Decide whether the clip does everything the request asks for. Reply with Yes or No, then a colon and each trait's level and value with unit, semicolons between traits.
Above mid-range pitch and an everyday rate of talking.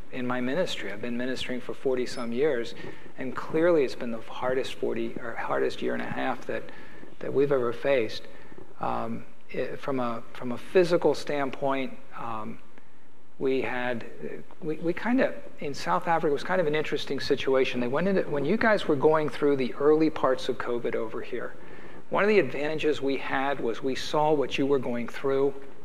No: low, 135 Hz; average, 195 wpm